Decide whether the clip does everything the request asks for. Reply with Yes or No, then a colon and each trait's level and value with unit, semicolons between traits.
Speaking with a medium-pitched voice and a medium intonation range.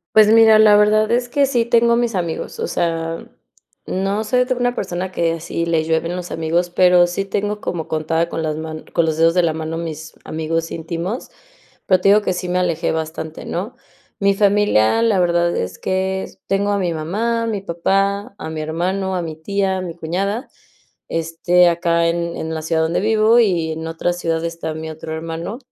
Yes: medium, 175 Hz; average, 3.7 semitones